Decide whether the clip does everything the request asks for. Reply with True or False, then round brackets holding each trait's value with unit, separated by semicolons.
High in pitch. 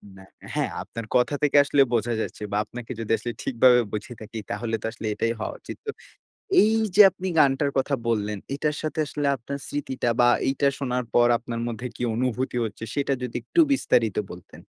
False (125 Hz)